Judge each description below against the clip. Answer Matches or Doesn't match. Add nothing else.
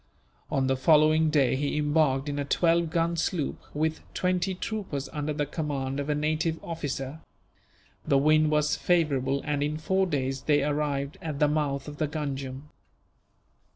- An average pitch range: Doesn't match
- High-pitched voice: Doesn't match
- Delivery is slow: Doesn't match